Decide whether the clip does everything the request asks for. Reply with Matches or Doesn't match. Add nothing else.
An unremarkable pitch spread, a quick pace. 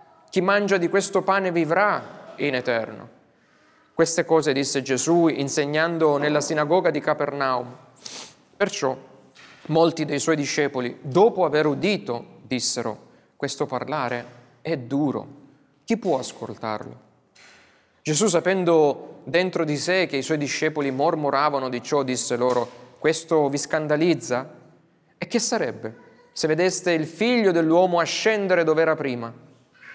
Doesn't match